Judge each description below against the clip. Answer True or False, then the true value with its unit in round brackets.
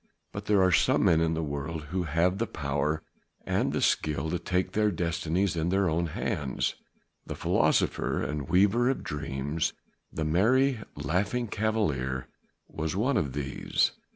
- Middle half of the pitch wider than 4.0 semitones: True (4.7 semitones)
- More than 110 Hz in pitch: False (85 Hz)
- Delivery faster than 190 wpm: False (155 wpm)